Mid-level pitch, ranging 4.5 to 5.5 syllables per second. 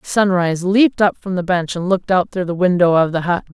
No: medium, 180 Hz; 6.0 syllables/s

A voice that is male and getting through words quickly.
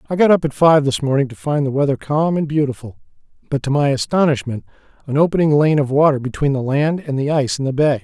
Yes: male; fast, 240 wpm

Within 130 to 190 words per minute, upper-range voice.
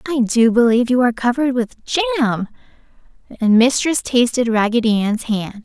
Yes: average, 150 wpm; high, 235 Hz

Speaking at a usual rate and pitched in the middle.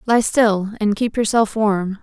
No: average, 180 wpm; high, 215 Hz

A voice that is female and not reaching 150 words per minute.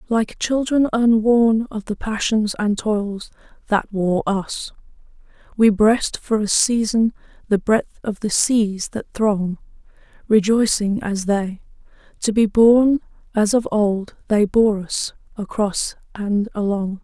Yes: female; slow, 135 wpm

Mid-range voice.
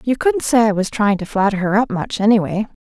No: high, 215 Hz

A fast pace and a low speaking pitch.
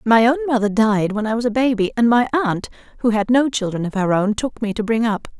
No: fast, 265 wpm; high, 225 Hz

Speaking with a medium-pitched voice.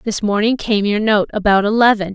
No: high, 210 Hz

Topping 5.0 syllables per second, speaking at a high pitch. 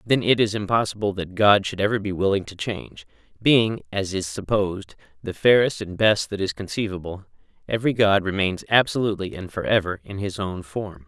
No: 5.5 syllables/s; low, 100 Hz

